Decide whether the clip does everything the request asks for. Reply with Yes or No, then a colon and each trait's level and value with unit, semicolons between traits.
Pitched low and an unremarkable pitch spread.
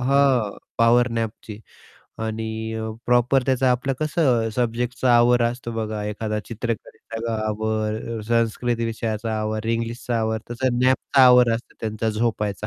No: low, 115 Hz; narrow, 1.9 semitones